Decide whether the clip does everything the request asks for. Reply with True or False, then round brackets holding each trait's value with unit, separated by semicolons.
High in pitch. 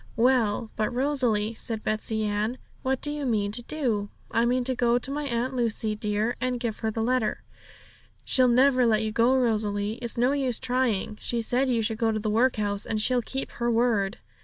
True (235 Hz)